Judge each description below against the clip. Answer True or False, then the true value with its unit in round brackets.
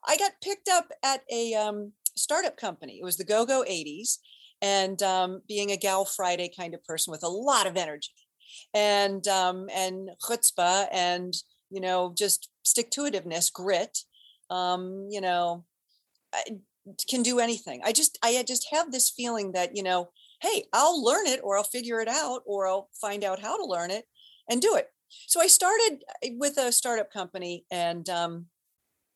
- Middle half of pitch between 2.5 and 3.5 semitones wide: False (5.1 semitones)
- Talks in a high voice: True (200 Hz)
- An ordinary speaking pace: True (175 wpm)